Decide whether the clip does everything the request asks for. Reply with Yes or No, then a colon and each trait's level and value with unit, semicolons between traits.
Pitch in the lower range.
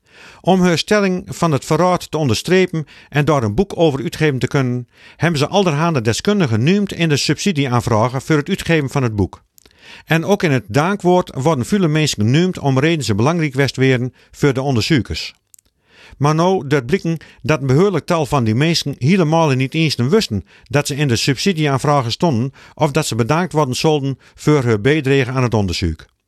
No: medium, 150 Hz